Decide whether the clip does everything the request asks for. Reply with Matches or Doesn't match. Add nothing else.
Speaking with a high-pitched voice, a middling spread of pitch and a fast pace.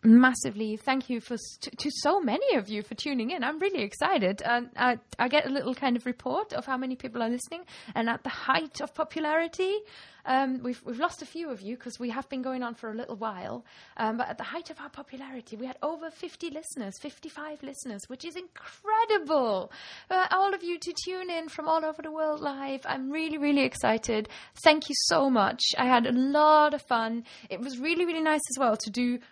Matches